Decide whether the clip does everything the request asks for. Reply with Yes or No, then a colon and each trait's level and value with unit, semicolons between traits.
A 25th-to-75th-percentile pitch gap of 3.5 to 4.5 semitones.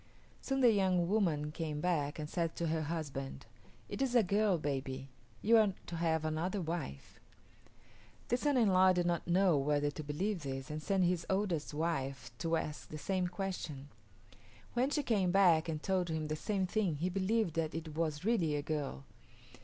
Yes: average, 4.2 semitones